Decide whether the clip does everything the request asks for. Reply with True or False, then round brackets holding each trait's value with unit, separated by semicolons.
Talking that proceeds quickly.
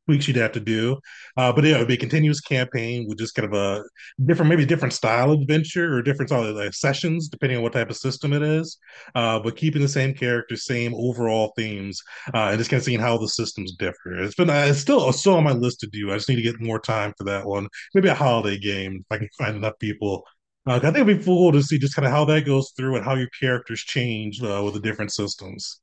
True (260 wpm)